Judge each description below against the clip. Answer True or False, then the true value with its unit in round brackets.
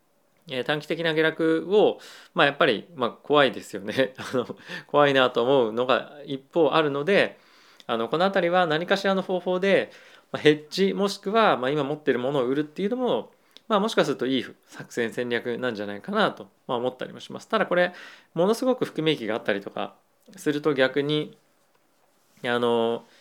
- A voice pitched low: False (155 Hz)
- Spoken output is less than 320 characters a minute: False (355 characters per minute)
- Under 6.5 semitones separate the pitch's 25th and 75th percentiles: False (7.1 semitones)